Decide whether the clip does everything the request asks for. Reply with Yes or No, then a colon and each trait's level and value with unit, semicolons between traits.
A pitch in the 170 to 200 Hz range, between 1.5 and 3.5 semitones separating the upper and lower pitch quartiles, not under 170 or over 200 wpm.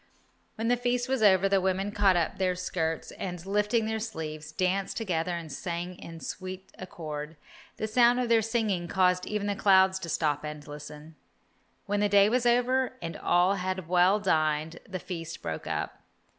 No: medium, 185 Hz; average, 3.9 semitones; average, 180 wpm